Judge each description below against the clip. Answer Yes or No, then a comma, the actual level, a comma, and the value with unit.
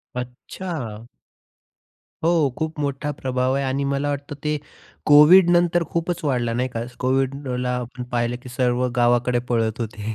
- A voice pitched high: No, low, 130 Hz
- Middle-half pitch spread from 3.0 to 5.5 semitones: Yes, average, 3.3 semitones